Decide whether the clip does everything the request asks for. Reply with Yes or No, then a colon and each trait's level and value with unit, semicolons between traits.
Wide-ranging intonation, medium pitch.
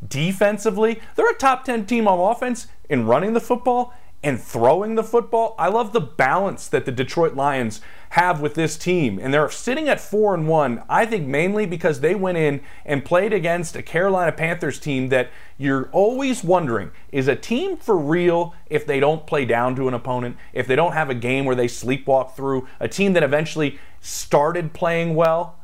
Yes: wide, 7.6 semitones; medium, 165 Hz